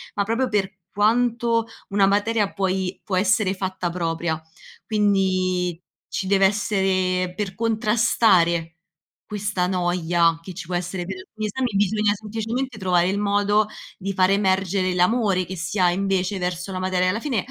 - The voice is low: No, high, 195 Hz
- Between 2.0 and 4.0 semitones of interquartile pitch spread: Yes, narrow, 2.5 semitones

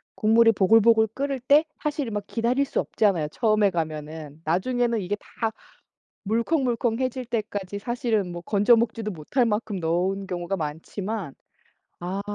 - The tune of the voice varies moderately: Yes, average, 4.5 semitones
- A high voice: Yes, high, 215 Hz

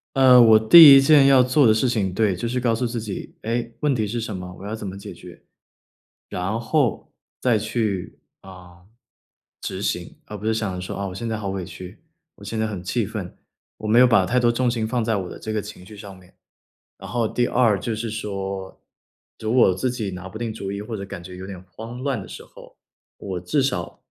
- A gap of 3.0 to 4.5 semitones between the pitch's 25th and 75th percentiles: Yes, average, 3.7 semitones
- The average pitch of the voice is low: Yes, low, 110 Hz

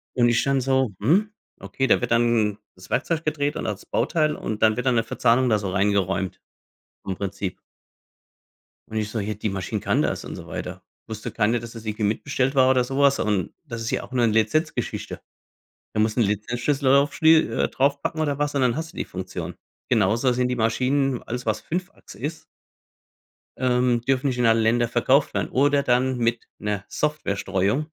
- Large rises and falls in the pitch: No, average, 4.2 semitones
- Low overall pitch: Yes, low, 120 Hz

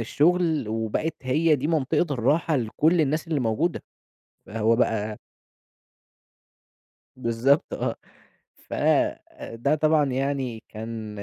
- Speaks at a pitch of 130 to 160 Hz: Yes, low, 135 Hz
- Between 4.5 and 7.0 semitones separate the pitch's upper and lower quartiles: Yes, wide, 5.4 semitones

